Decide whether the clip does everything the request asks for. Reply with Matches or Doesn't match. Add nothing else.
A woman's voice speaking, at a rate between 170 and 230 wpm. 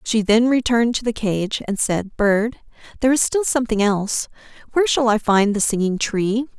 Matches